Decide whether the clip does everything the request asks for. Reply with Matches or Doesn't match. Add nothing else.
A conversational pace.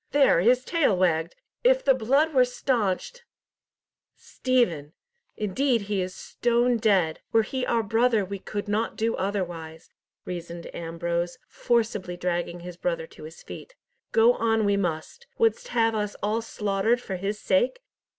Matches